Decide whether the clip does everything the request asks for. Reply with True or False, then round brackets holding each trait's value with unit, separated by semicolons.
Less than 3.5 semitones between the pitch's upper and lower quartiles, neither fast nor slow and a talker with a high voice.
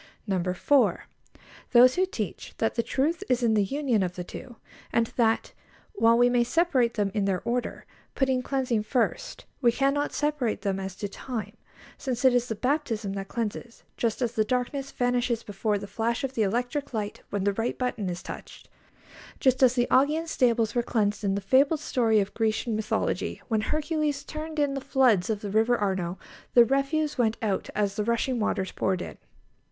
False (4.0 semitones; 190 wpm; 235 Hz)